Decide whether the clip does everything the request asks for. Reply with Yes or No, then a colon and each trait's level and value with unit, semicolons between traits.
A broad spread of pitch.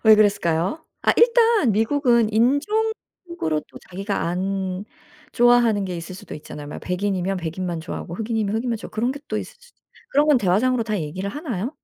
Yes: wide, 5.7 semitones